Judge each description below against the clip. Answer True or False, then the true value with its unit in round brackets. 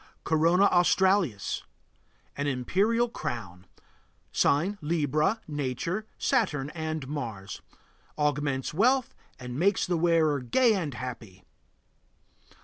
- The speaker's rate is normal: False (95 wpm)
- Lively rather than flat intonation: True (6.3 semitones)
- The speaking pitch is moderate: True (155 Hz)